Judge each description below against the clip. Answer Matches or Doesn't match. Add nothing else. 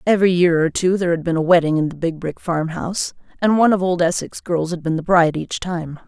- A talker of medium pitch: Matches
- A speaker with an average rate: Doesn't match